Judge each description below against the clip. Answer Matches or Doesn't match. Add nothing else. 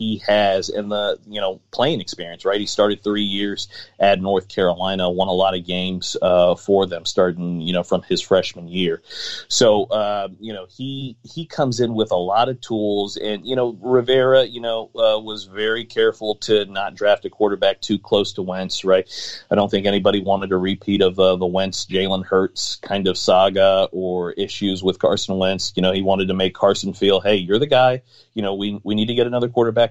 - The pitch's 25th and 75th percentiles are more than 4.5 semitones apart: Doesn't match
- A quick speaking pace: Matches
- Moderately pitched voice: Doesn't match